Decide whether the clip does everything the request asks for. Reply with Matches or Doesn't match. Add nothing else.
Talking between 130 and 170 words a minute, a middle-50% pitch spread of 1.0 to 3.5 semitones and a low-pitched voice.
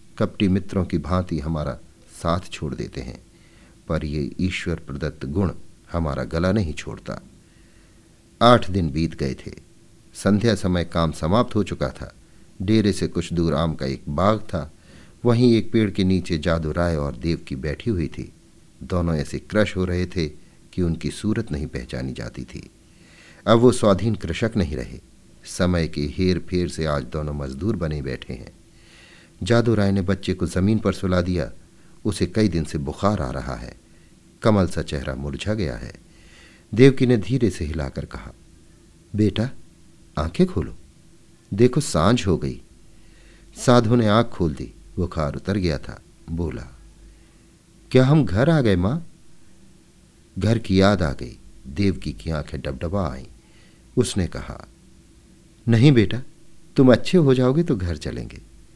Doesn't match